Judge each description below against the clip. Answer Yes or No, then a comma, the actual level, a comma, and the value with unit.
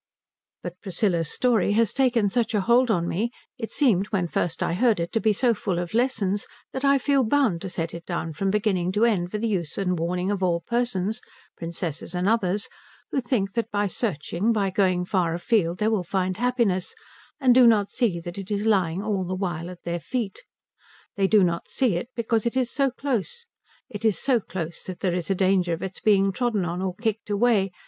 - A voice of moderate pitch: No, high, 200 Hz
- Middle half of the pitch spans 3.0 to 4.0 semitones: No, average, 4.4 semitones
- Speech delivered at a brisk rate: Yes, fast, 215 wpm